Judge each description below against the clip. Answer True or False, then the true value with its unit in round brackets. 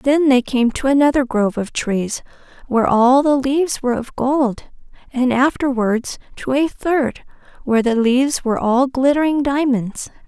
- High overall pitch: True (260 Hz)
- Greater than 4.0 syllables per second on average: True (4.7 syllables/s)